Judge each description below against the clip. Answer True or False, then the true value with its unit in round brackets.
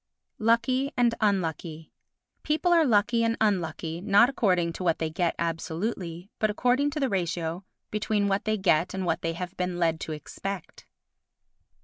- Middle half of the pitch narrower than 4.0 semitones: False (5.3 semitones)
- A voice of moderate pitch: False (195 Hz)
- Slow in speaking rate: False (160 wpm)